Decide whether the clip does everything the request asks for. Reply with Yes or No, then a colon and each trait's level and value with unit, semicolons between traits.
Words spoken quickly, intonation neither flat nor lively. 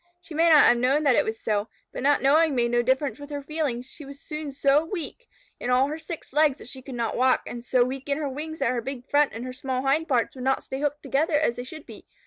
Yes: fast, 280 wpm; average, 3.0 semitones